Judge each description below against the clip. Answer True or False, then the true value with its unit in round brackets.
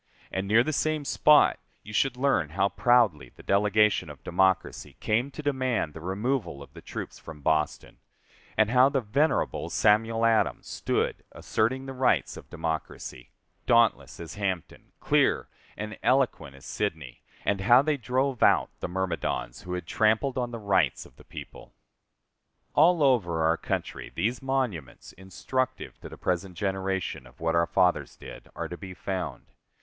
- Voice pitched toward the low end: True (105 Hz)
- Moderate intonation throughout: False (6.3 semitones)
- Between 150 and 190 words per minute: True (160 wpm)